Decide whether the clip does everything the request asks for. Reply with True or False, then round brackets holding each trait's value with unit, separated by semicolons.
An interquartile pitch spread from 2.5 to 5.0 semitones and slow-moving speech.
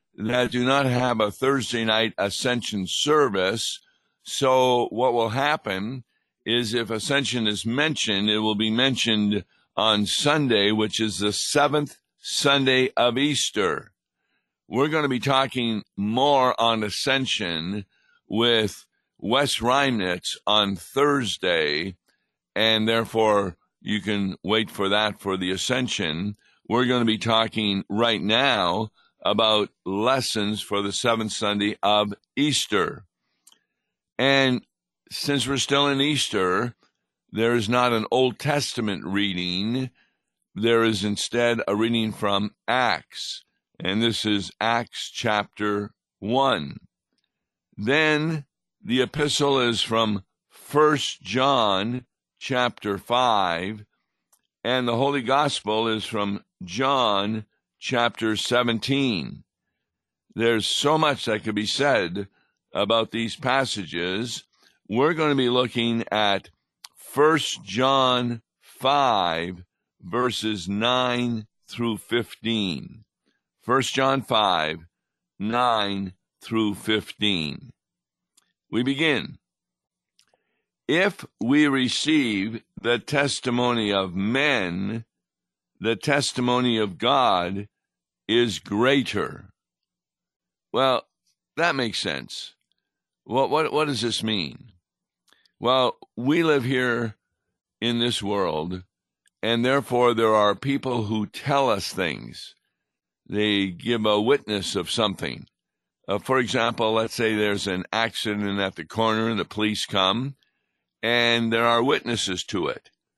True (3.4 semitones; 110 wpm)